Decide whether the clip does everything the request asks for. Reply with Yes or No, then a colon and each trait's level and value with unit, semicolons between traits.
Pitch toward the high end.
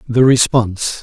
No: low, 115 Hz